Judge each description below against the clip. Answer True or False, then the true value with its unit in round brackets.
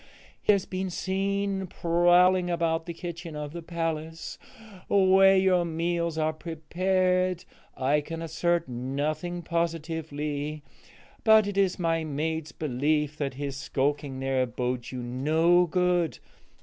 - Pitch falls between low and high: True (165 Hz)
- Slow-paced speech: True (125 wpm)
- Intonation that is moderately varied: True (3.2 semitones)